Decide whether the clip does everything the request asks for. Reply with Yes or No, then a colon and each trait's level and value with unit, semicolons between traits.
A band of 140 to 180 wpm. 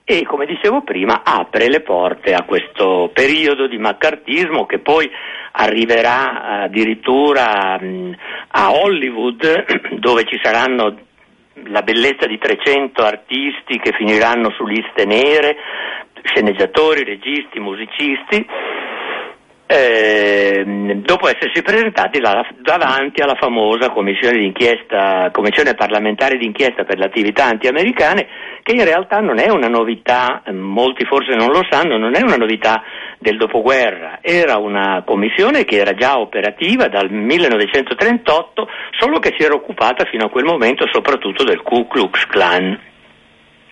No: average, 125 wpm